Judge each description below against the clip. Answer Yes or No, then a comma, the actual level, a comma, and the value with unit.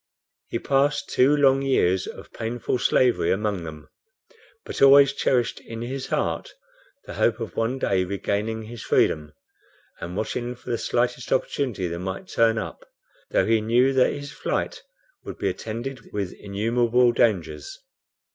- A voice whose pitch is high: No, low, 115 Hz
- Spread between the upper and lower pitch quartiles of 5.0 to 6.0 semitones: No, average, 4.1 semitones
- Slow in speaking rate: No, average, 150 wpm